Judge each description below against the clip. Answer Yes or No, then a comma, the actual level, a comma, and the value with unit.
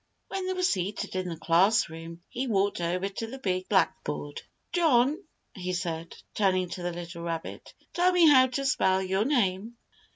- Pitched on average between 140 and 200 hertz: Yes, high, 190 Hz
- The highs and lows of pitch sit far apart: Yes, wide, 6.7 semitones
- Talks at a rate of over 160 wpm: Yes, average, 170 wpm